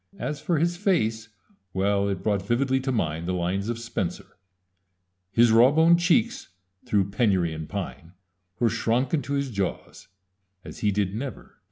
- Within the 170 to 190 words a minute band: No, average, 160 wpm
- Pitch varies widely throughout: Yes, wide, 5.8 semitones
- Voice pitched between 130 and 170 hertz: No, low, 110 Hz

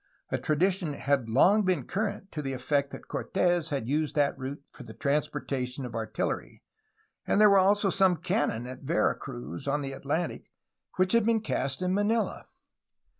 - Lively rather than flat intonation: Yes, wide, 5.9 semitones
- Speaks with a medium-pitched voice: Yes, medium, 150 Hz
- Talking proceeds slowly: No, average, 175 wpm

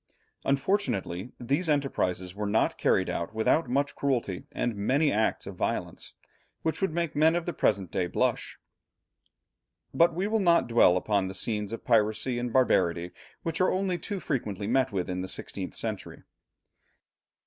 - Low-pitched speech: Yes, low, 120 Hz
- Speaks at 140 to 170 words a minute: Yes, average, 160 wpm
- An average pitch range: No, wide, 8.1 semitones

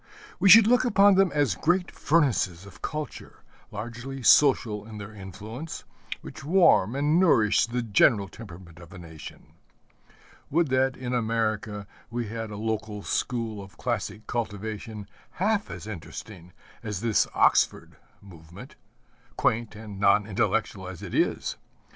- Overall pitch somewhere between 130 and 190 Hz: No, low, 110 Hz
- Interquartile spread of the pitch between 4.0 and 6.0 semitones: Yes, average, 4.6 semitones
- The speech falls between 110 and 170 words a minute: Yes, average, 140 wpm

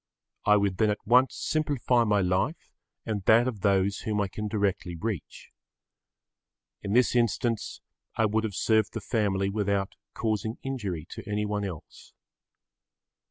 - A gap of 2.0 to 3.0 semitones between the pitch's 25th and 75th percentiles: Yes, narrow, 2.4 semitones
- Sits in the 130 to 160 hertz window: No, low, 105 Hz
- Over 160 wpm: No, average, 145 wpm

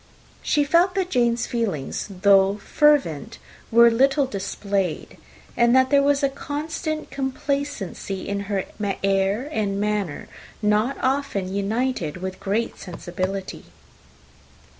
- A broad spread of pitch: Yes, wide, 6.0 semitones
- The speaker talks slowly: Yes, slow, 115 wpm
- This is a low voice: No, high, 220 Hz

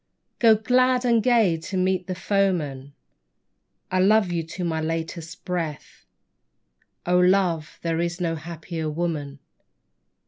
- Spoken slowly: Yes, slow, 130 wpm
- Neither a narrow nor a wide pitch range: Yes, average, 3.0 semitones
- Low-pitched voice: No, medium, 175 Hz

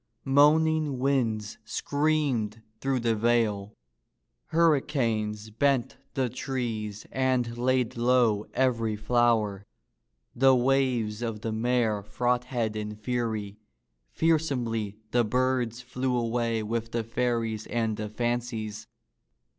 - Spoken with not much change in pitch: No, average, 3.0 semitones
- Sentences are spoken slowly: Yes, slow, 105 wpm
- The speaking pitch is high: No, low, 120 Hz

